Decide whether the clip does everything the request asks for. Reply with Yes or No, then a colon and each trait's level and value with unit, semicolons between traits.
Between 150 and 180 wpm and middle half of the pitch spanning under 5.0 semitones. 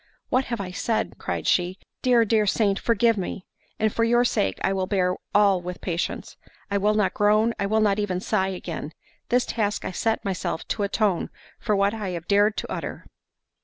No: average, 190 wpm; average, 2.7 semitones